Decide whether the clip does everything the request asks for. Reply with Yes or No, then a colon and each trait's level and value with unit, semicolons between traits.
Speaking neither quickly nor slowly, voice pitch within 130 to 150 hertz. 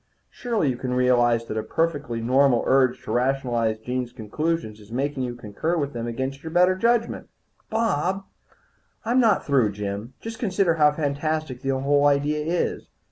Yes: average, 170 wpm; medium, 140 Hz